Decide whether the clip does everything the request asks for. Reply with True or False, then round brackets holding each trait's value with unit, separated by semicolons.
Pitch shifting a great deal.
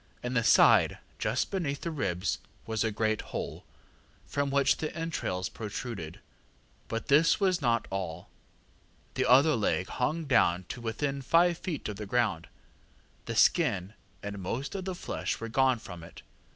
True (6.2 semitones)